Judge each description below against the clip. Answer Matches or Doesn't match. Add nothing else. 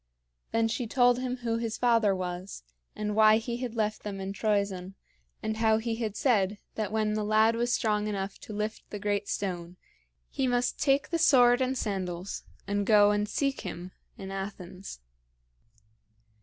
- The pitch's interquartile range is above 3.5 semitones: Doesn't match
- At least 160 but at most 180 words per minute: Matches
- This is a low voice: Doesn't match